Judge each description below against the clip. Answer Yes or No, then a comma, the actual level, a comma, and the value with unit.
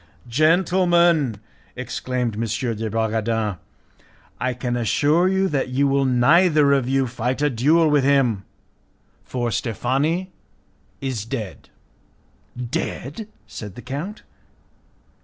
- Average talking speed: No, slow, 110 wpm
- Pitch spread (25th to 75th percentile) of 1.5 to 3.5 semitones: No, average, 4.5 semitones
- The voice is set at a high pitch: No, low, 130 Hz